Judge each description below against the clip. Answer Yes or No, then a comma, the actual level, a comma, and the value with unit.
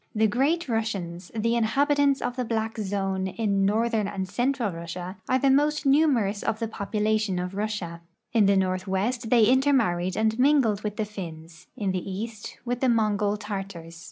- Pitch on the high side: Yes, high, 215 Hz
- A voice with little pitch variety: No, average, 3.8 semitones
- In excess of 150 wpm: Yes, average, 175 wpm